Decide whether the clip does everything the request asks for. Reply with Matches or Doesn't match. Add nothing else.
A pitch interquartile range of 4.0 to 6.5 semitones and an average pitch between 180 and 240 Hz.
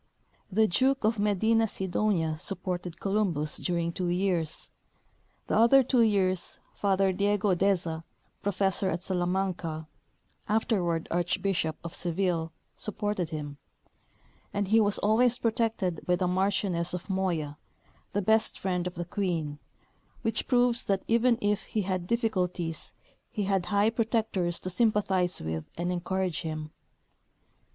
Doesn't match